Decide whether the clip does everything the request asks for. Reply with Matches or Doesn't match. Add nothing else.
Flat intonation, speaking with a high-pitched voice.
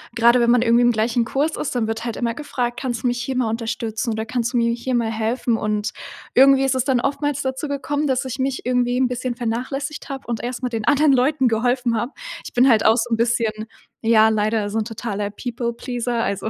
Matches